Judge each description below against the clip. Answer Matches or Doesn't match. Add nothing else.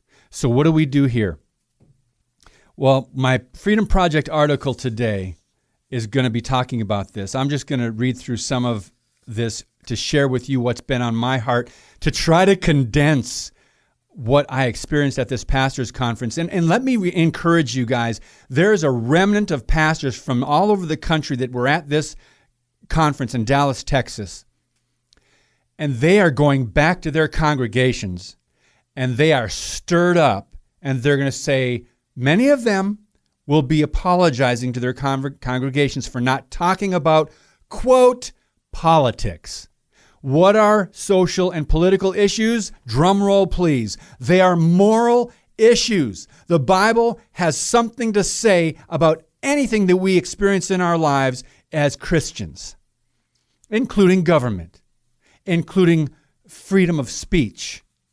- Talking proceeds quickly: Doesn't match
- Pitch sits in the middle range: Matches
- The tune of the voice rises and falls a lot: Matches